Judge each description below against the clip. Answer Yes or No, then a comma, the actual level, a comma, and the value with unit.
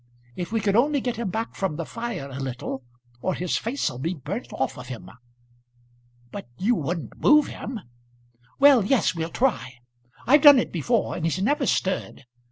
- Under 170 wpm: No, average, 175 wpm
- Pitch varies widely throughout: Yes, wide, 7.7 semitones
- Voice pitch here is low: No, high, 195 Hz